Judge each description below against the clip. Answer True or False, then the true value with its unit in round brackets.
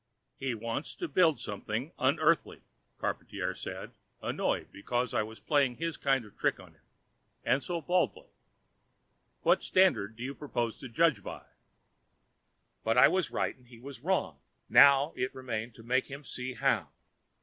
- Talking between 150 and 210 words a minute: True (160 wpm)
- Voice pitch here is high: False (130 Hz)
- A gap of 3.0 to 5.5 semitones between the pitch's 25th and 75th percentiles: True (4.2 semitones)